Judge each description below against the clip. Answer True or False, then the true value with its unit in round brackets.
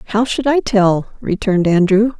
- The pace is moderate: True (165 wpm)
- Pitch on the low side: False (210 Hz)